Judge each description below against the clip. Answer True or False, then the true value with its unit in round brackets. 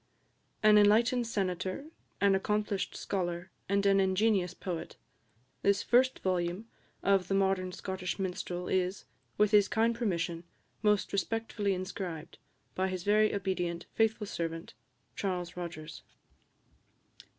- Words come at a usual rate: False (115 wpm)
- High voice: True (195 Hz)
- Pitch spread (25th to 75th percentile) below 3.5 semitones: True (2.7 semitones)